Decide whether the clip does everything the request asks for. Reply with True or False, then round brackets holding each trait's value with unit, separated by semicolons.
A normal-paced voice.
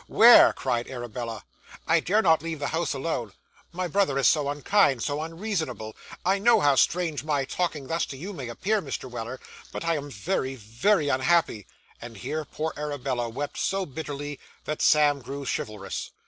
True (175 wpm)